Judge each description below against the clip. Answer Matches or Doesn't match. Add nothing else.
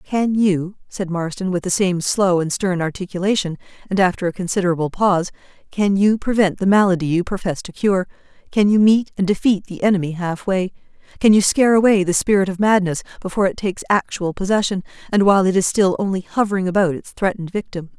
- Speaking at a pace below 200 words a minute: Matches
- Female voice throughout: Matches